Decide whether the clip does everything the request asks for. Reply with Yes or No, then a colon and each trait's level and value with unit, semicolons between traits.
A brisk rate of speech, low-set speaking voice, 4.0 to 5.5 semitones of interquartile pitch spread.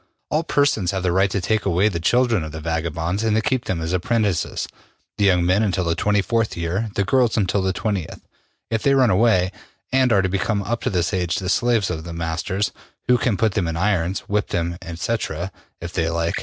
Yes: fast, 220 wpm; very low, 95 Hz; average, 4.4 semitones